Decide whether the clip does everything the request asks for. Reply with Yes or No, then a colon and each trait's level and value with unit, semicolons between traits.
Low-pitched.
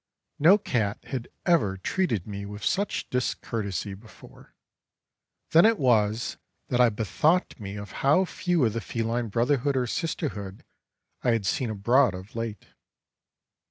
Yes: low, 115 Hz